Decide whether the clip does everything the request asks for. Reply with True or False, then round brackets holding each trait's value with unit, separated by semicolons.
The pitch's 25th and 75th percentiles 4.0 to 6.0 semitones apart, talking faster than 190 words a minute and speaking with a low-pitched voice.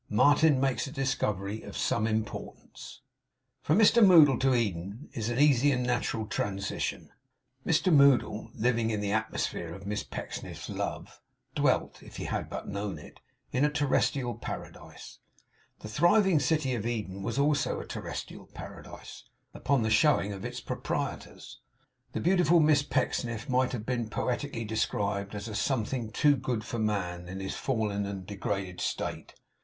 False (5.3 semitones; 155 wpm; 115 Hz)